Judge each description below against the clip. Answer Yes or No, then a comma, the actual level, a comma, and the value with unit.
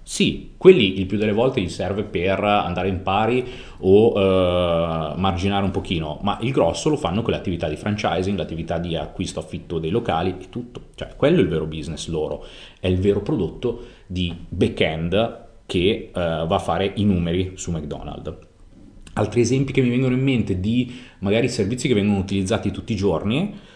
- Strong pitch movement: No, average, 4.3 semitones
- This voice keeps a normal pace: No, fast, 185 wpm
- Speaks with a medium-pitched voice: No, very low, 95 Hz